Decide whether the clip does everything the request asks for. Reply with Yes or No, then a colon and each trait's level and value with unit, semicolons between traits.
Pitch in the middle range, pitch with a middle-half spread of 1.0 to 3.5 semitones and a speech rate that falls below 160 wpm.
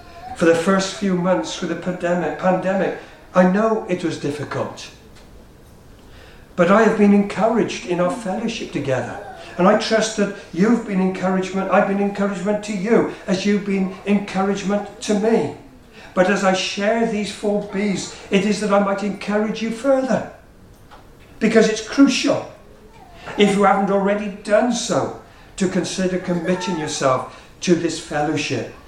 No: high, 195 Hz; average, 2.7 semitones; average, 150 wpm